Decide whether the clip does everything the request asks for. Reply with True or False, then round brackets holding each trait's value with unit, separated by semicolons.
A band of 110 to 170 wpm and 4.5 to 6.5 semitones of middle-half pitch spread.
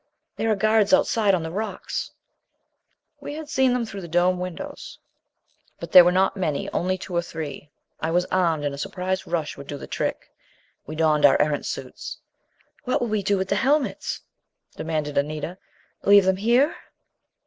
False (180 wpm; 5.0 semitones)